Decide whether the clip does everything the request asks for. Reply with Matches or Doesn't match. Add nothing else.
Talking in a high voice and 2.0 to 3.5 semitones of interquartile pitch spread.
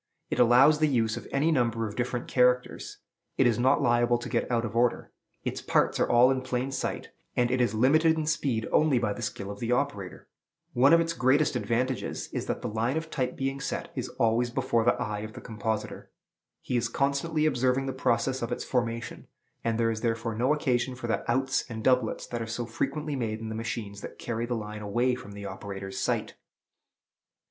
Doesn't match